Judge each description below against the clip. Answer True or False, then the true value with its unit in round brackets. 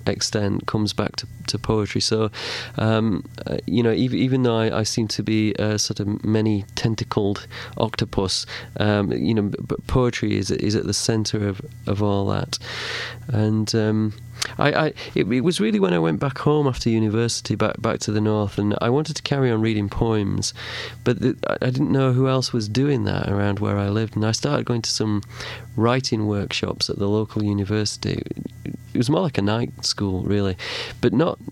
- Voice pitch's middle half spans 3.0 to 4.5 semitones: False (2.5 semitones)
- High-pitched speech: False (110 Hz)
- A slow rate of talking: False (195 wpm)